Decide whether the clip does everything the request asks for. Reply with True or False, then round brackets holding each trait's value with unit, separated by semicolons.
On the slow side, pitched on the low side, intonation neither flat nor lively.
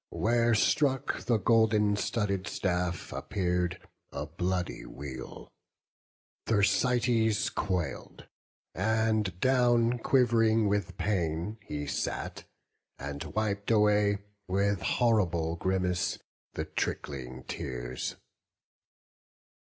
True (85 wpm; 100 Hz; 4.2 semitones)